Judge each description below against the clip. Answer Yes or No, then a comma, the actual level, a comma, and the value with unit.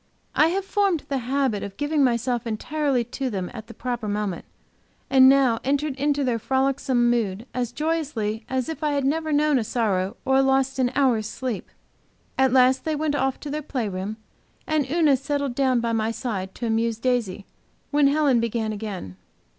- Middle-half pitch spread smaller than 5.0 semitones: Yes, average, 3.9 semitones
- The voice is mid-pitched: No, very high, 255 Hz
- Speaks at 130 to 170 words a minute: No, average, 185 wpm